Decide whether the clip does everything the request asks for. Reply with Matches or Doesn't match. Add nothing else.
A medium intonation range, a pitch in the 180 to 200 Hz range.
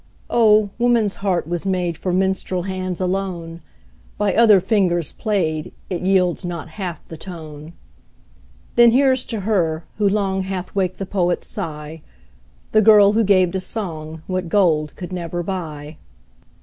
Matches